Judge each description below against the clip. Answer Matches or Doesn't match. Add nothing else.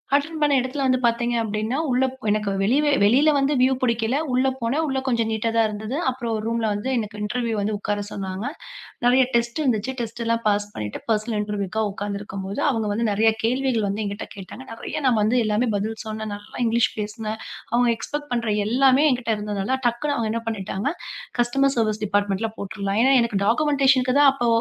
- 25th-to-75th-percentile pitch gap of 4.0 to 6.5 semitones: Doesn't match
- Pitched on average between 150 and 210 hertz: Doesn't match